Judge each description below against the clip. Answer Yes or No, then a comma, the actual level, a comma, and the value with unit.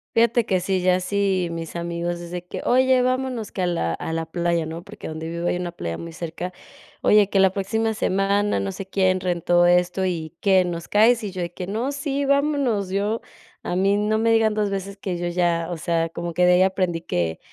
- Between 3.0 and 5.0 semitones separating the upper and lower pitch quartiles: Yes, average, 3.3 semitones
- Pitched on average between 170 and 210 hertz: Yes, medium, 185 Hz